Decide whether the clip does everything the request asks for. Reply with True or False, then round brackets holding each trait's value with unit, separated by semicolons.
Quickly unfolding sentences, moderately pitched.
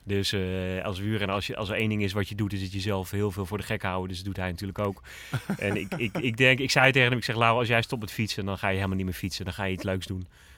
False (340 wpm; 100 Hz)